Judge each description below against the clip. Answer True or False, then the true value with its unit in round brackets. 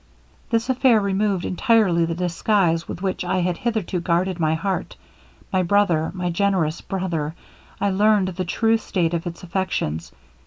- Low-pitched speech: False (185 Hz)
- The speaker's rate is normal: True (150 wpm)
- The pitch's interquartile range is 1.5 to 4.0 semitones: True (3.1 semitones)